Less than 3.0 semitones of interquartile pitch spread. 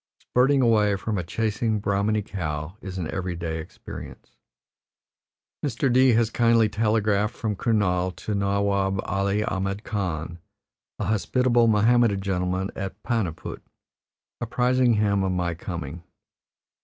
No: average, 3.3 semitones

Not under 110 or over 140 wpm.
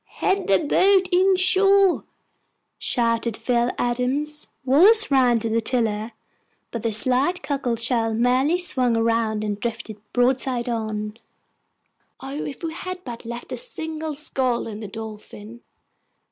Yes: slow, 135 wpm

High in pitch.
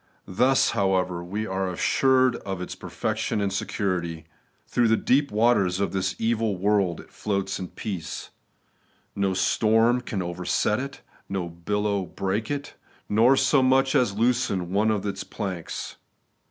No: low, 100 Hz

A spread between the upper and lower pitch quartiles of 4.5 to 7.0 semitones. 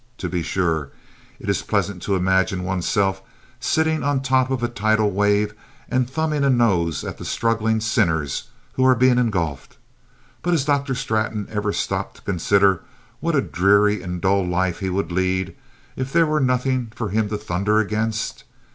Yes: average, 5.1 semitones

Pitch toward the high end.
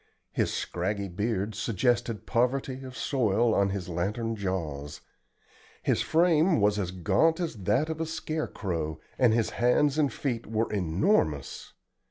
No: low, 110 Hz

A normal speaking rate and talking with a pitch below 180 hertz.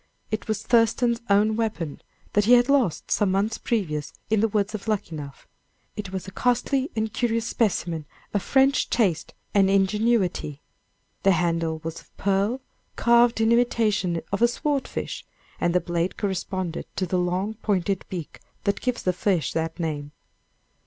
No: average, 160 wpm; high, 200 Hz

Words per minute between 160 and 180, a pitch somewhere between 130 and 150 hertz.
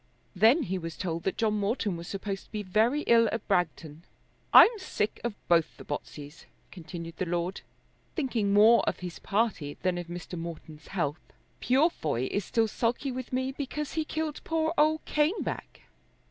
No: average, 170 wpm; high, 205 Hz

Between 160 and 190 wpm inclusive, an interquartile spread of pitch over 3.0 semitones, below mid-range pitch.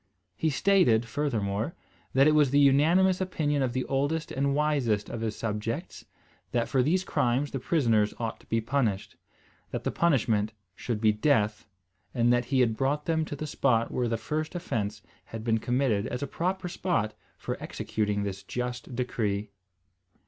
Yes: average, 170 wpm; average, 5.0 semitones; low, 125 Hz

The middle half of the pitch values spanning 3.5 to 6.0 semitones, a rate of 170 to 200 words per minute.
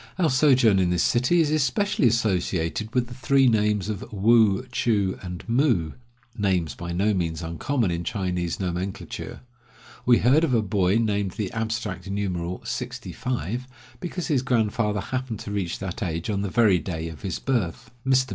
Yes: average, 5.2 semitones; average, 175 wpm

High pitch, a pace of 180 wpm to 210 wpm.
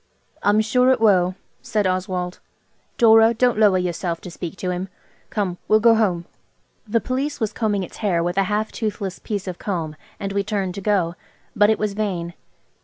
Yes: high, 200 Hz; average, 185 wpm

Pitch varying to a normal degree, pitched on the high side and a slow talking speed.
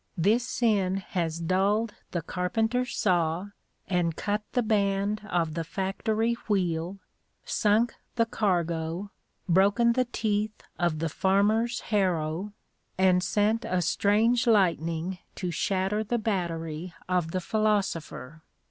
Yes: average, 3.9 semitones; high, 195 Hz; slow, 120 wpm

